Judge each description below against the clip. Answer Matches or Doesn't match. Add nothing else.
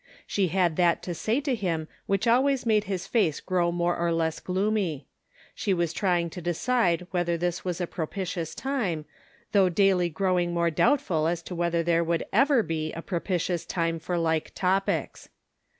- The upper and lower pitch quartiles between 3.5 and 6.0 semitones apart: Doesn't match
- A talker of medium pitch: Matches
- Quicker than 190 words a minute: Doesn't match